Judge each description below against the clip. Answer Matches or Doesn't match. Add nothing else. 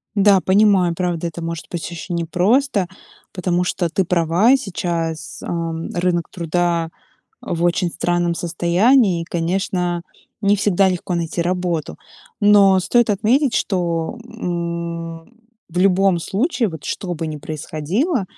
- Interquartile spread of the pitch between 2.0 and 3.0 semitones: Matches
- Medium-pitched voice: Matches